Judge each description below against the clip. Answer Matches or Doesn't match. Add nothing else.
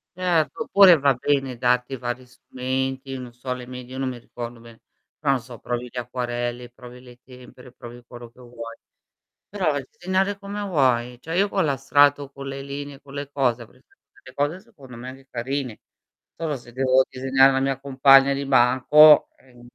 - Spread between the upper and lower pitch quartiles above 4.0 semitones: Doesn't match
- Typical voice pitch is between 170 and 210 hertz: Doesn't match